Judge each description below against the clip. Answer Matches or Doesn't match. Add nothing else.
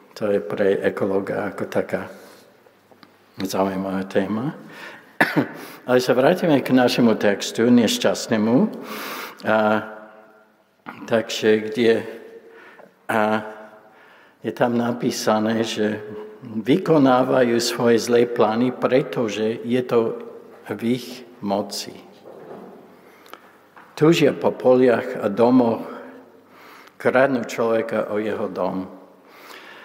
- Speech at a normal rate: Doesn't match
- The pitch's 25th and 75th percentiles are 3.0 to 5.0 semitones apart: Doesn't match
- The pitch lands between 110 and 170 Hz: Matches